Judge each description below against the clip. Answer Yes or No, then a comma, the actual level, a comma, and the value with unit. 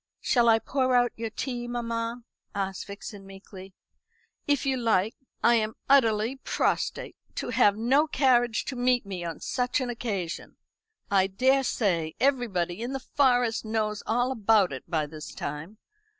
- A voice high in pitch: Yes, high, 225 Hz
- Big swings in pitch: No, average, 4.2 semitones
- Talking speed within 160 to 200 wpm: No, average, 150 wpm